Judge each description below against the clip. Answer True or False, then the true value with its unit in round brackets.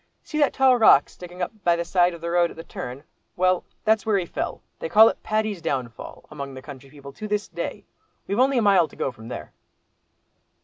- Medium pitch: True (175 Hz)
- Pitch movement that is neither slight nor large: False (6.8 semitones)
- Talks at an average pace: False (225 wpm)